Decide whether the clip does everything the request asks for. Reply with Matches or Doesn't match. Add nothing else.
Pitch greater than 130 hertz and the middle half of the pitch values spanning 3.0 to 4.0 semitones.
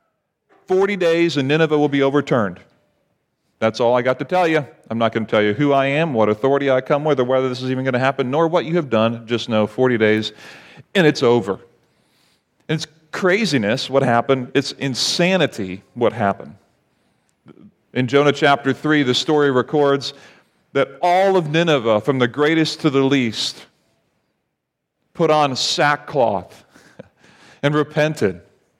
Matches